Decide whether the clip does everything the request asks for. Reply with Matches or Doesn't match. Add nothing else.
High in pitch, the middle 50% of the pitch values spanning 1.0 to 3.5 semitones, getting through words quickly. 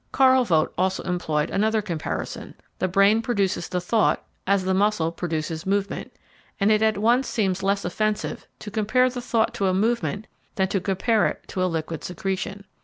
Doesn't match